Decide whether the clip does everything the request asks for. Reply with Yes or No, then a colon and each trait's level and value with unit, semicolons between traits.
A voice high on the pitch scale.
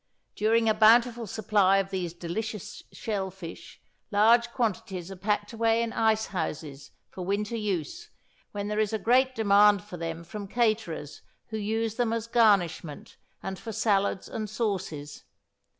Yes: high, 210 Hz